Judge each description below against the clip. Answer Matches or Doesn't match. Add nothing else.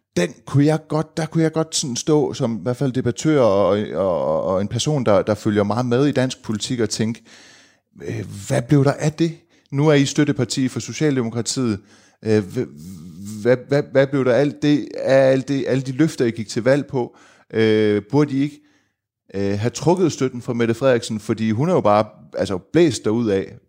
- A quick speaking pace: Doesn't match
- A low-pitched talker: Matches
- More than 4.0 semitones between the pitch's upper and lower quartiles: Matches